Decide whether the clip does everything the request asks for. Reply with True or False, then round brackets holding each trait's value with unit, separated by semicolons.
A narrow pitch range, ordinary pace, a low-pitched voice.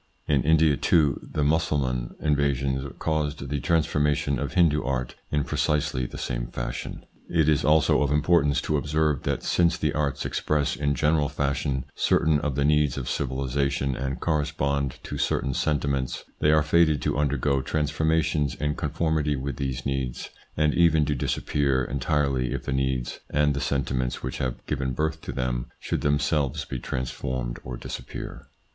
True (2.3 semitones; 165 wpm; 70 Hz)